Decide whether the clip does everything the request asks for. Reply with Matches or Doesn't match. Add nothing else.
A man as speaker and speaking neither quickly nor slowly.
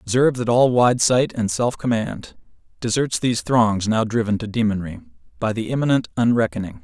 Matches